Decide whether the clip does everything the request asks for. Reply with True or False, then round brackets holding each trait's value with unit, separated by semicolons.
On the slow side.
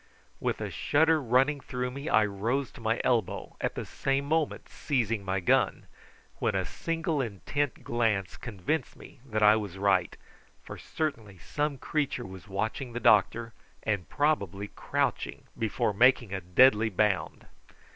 False (150 wpm)